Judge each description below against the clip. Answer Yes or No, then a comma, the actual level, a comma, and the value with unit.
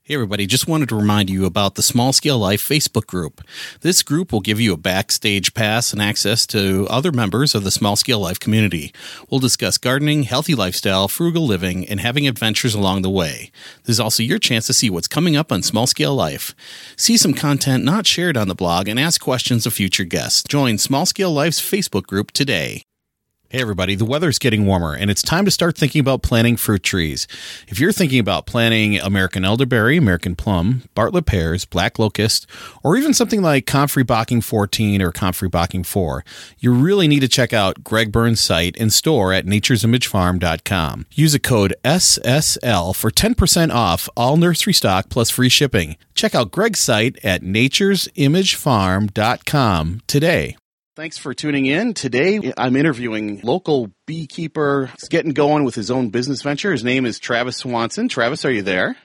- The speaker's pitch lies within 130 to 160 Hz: No, low, 120 Hz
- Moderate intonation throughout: No, wide, 6.1 semitones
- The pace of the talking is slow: No, average, 185 wpm